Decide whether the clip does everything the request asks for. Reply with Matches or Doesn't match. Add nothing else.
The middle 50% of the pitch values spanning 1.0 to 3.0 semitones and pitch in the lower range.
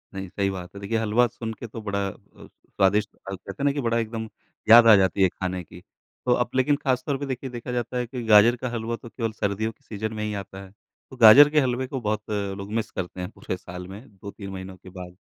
Doesn't match